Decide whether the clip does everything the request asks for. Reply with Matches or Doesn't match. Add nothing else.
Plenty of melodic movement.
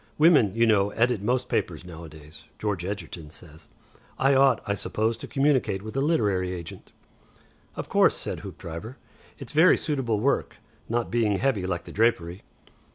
Matches